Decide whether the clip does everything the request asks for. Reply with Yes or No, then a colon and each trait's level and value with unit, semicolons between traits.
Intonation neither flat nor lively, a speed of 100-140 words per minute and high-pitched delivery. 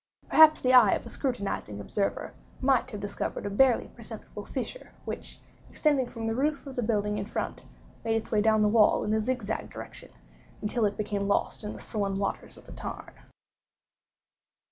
No: average, 3.7 semitones; average, 185 wpm; high, 220 Hz